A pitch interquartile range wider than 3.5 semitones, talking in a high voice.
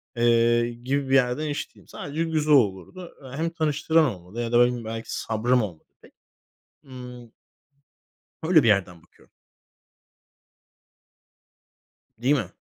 No: average, 4.2 semitones; low, 125 Hz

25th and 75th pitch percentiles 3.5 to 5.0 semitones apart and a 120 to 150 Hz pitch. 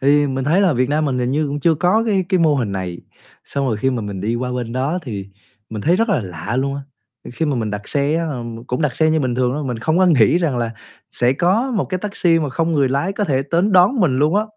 No: wide, 5.4 semitones; medium, 140 Hz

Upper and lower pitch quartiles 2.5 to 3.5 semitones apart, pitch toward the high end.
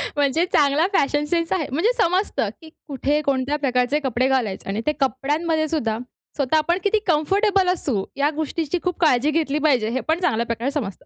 No: average, 4.1 semitones; very high, 290 Hz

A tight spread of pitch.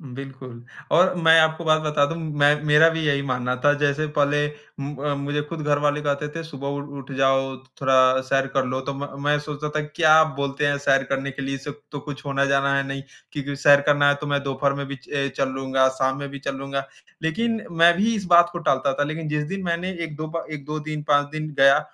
Yes: narrow, 2.0 semitones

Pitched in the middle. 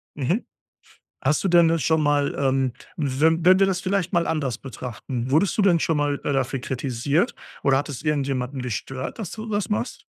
Yes: medium, 145 Hz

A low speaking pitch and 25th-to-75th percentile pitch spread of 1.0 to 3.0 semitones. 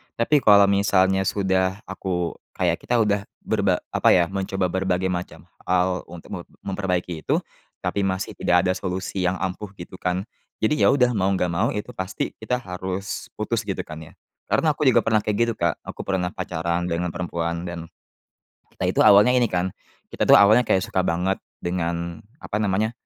Yes: very low, 95 Hz; narrow, 2.6 semitones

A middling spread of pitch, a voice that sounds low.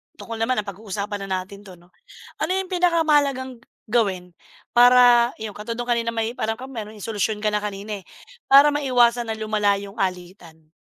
No: average, 3.4 semitones; high, 220 Hz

